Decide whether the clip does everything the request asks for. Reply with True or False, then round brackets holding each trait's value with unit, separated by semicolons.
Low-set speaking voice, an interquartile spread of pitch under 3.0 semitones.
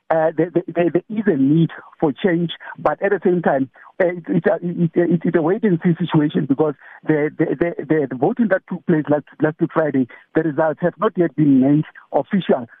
False (165 Hz; 2.6 semitones)